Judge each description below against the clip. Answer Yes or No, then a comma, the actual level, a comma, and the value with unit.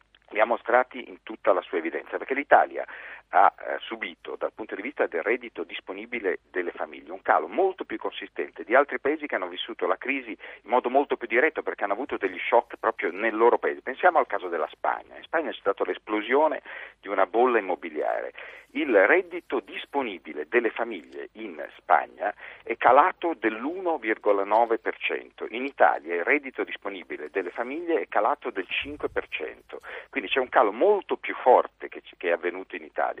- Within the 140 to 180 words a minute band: Yes, fast, 170 wpm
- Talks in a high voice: Yes, very high, 375 Hz